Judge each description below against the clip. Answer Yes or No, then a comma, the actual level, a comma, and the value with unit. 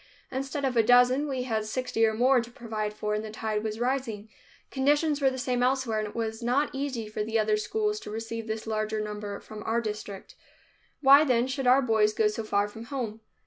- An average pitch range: Yes, average, 3.4 semitones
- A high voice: Yes, high, 230 Hz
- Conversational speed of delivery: No, fast, 220 wpm